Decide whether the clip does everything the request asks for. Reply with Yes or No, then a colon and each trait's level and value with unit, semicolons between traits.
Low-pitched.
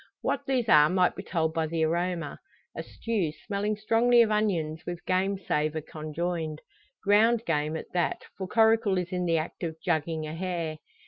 No: medium, 175 Hz